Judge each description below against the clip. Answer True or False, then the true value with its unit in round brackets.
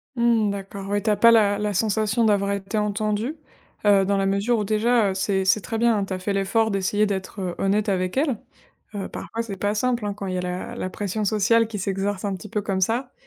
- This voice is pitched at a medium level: False (205 Hz)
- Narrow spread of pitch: True (2.2 semitones)